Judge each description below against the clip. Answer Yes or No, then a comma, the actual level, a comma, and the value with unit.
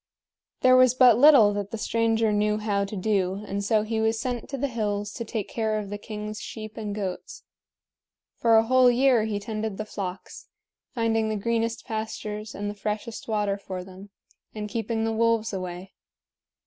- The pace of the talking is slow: No, average, 185 wpm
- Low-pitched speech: No, high, 215 Hz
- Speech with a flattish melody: Yes, narrow, 1.8 semitones